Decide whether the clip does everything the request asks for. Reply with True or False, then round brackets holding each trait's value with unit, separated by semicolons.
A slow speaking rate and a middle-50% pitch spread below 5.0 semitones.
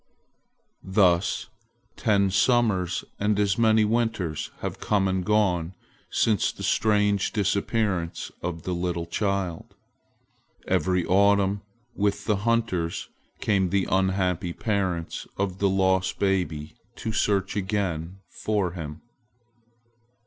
True (110 wpm; 2.5 semitones)